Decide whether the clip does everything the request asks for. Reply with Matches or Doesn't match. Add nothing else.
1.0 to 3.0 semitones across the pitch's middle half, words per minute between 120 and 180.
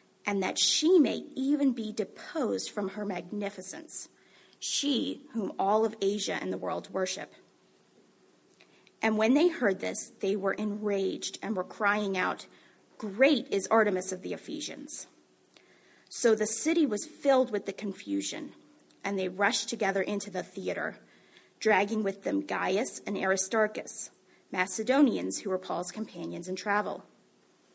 Matches